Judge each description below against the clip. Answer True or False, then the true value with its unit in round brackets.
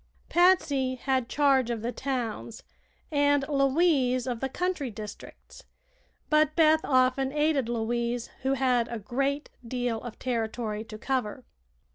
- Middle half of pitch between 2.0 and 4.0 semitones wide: True (3.1 semitones)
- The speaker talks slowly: True (130 wpm)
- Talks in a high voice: True (255 Hz)